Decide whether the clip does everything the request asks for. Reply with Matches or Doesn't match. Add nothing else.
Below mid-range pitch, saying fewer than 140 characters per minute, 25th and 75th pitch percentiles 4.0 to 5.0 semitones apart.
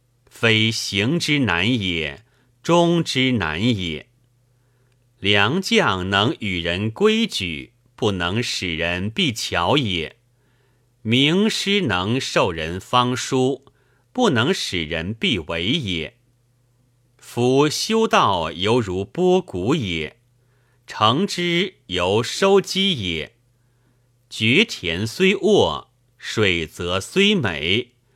Matches